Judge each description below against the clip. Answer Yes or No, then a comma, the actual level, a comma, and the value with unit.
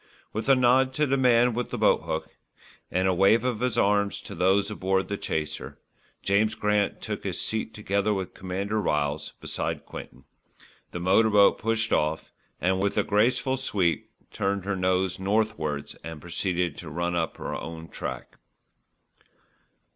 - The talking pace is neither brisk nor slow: Yes, average, 160 wpm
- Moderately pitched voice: No, low, 100 Hz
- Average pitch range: Yes, average, 3.7 semitones